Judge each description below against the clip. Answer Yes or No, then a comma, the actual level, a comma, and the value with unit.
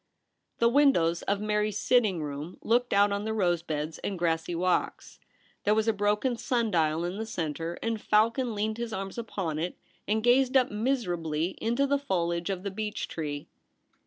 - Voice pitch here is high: Yes, high, 205 Hz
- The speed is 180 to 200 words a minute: Yes, average, 185 wpm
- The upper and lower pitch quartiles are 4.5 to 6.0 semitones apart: Yes, average, 5.0 semitones